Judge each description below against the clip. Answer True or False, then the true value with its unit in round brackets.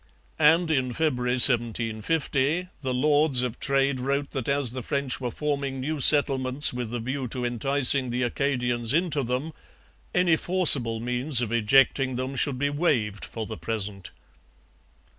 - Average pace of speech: True (150 wpm)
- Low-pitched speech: True (130 Hz)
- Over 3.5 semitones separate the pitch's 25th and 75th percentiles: False (2.8 semitones)